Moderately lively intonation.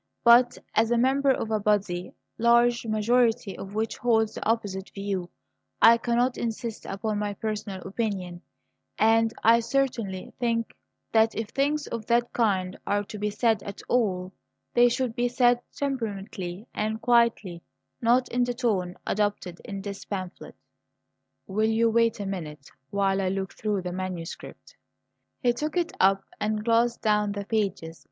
Yes: average, 3.3 semitones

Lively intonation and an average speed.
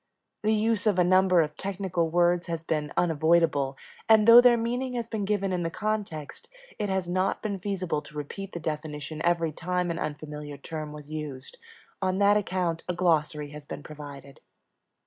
No: average, 4.5 semitones; average, 180 wpm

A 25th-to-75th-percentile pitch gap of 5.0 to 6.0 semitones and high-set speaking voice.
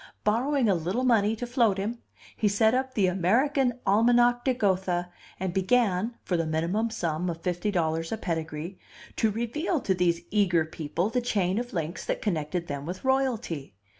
Yes: wide, 5.6 semitones; high, 200 Hz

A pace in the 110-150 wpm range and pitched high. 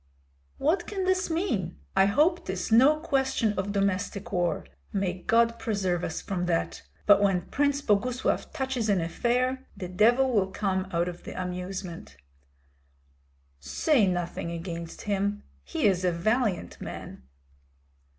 Yes: slow, 135 wpm; high, 200 Hz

